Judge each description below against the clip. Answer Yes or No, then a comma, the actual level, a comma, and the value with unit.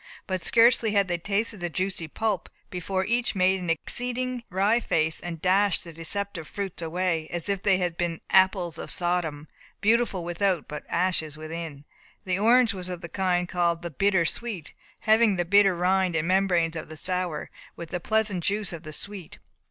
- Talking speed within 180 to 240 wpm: Yes, average, 185 wpm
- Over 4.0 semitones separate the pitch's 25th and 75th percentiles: No, average, 3.1 semitones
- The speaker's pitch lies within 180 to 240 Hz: Yes, medium, 185 Hz